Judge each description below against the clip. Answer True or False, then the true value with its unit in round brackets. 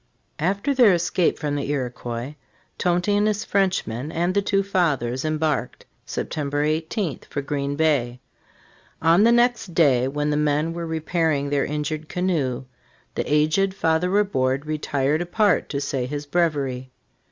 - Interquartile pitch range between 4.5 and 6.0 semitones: False (4.1 semitones)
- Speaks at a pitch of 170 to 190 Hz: False (155 Hz)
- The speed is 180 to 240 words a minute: False (150 wpm)